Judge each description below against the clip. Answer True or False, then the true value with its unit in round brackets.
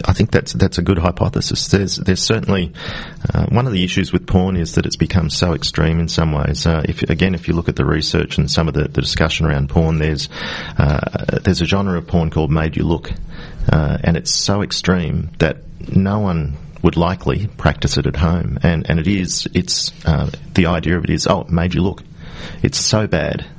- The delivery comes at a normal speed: False (210 wpm)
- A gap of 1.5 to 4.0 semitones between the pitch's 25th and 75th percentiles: True (2.7 semitones)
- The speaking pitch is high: False (85 Hz)